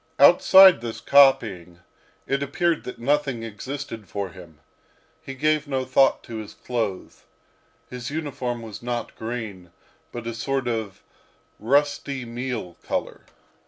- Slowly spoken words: Yes, slow, 125 wpm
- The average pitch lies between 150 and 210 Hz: No, low, 120 Hz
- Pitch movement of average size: Yes, average, 3.9 semitones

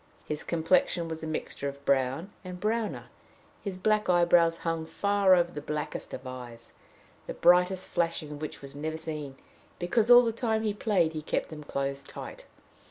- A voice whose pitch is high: No, medium, 165 Hz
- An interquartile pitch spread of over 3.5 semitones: Yes, average, 4.2 semitones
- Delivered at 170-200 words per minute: Yes, average, 175 wpm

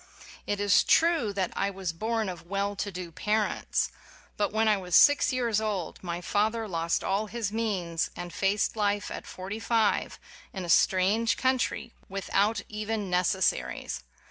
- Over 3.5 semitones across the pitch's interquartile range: No, average, 2.9 semitones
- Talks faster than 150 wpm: Yes, average, 165 wpm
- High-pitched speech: Yes, high, 205 Hz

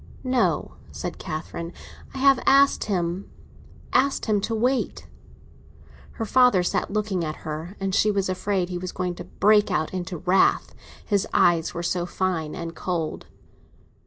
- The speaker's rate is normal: Yes, average, 150 wpm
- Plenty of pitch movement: No, average, 3.6 semitones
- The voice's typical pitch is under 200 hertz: Yes, medium, 185 Hz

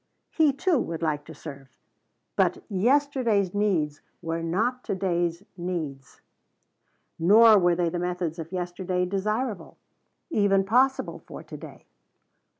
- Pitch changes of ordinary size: Yes, average, 4.4 semitones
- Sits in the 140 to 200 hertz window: Yes, medium, 185 Hz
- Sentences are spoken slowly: Yes, slow, 125 wpm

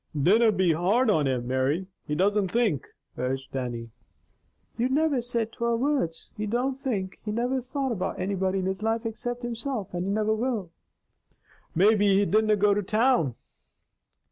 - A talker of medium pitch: No, high, 210 Hz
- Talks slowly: No, average, 165 wpm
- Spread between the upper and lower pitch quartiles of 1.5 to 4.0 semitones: No, average, 4.7 semitones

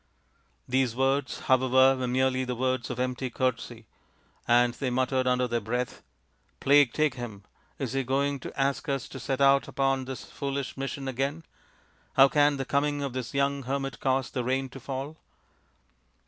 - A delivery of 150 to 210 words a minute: Yes, average, 175 wpm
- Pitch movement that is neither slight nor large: No, narrow, 1.6 semitones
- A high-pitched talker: No, low, 130 Hz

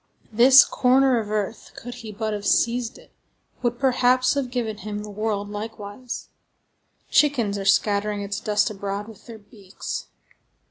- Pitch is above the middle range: Yes, high, 215 Hz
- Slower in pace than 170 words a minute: Yes, average, 150 wpm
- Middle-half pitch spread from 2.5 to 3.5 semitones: Yes, average, 3.0 semitones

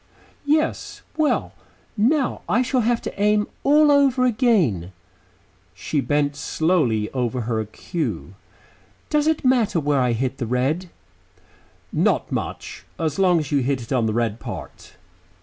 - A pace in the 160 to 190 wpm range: No, average, 145 wpm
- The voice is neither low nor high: Yes, medium, 155 Hz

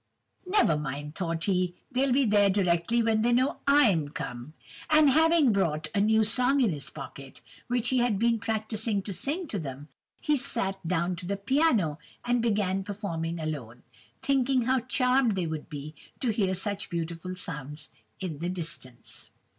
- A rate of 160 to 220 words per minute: Yes, average, 170 wpm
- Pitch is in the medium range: No, high, 200 Hz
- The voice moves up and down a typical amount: No, wide, 6.8 semitones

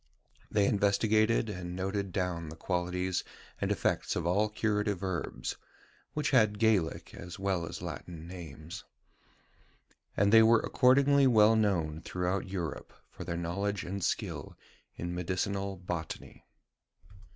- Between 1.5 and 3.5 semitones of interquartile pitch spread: Yes, average, 3.2 semitones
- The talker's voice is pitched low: Yes, very low, 95 Hz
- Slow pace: Yes, slow, 130 wpm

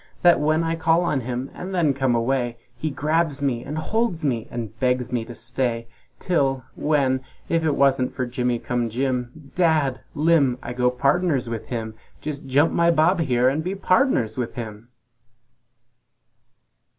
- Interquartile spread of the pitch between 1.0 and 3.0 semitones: No, average, 4.5 semitones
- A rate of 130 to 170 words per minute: Yes, average, 165 wpm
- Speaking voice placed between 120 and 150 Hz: Yes, low, 135 Hz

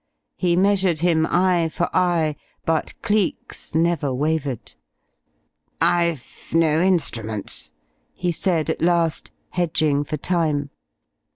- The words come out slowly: Yes, slow, 105 wpm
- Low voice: No, medium, 165 Hz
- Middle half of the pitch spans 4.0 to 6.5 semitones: No, narrow, 2.4 semitones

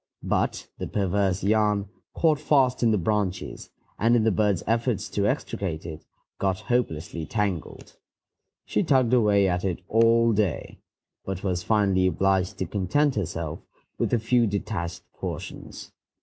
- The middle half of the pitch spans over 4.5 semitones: No, average, 3.6 semitones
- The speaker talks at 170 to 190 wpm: No, average, 145 wpm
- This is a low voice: Yes, low, 100 Hz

